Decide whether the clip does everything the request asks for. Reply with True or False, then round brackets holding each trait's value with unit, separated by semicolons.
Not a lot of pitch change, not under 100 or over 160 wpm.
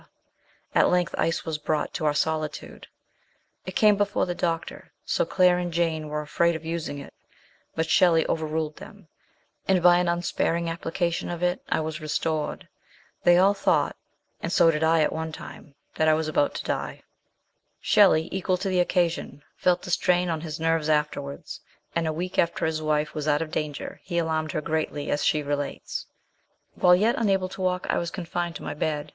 False (2.3 semitones; 195 wpm)